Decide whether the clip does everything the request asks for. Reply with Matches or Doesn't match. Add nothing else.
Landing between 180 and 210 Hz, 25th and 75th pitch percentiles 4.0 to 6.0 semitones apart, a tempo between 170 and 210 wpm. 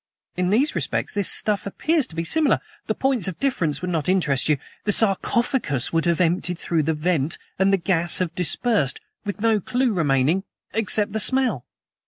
Matches